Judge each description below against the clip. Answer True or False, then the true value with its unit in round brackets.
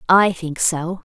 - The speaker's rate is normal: True (160 wpm)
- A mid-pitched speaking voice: True (175 Hz)